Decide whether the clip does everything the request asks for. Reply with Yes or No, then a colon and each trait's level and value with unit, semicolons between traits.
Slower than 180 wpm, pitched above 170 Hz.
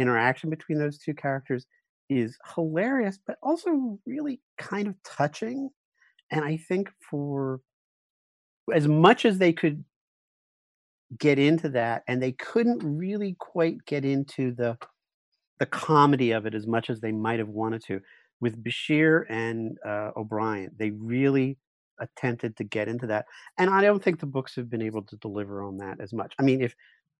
No: average, 165 wpm; low, 135 Hz